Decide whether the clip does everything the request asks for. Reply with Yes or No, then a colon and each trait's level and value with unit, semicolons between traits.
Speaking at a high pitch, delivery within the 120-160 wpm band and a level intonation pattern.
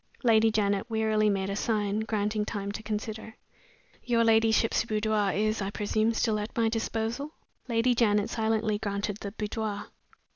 Yes: high, 220 Hz; average, 150 wpm; narrow, 1.3 semitones